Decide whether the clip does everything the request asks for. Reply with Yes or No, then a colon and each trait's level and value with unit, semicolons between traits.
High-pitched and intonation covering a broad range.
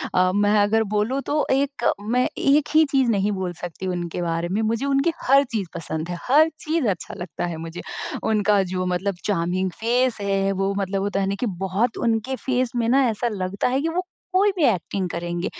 Yes: high, 205 Hz; wide, 5.8 semitones